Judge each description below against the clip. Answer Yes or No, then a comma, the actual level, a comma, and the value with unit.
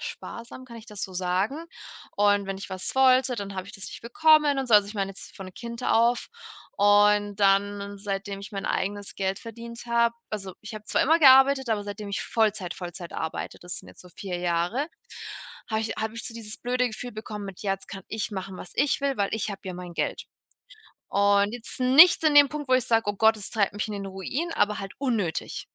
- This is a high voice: Yes, high, 210 Hz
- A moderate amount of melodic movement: Yes, average, 3.3 semitones